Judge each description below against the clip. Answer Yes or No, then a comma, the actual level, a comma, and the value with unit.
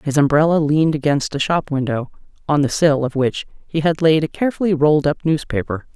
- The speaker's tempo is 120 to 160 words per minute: No, average, 200 wpm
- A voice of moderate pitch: Yes, medium, 150 Hz